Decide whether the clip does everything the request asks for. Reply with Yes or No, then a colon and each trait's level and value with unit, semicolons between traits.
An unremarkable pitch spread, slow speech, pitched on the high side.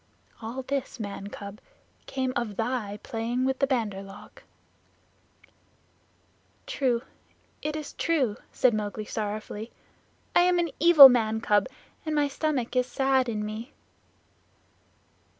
Yes: average, 4.2 semitones; slow, 125 wpm; high, 245 Hz